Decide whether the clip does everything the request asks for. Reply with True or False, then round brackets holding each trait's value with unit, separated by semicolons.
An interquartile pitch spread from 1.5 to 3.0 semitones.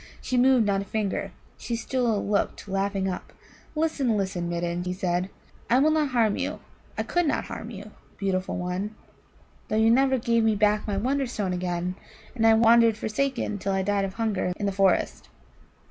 False (3.6 semitones)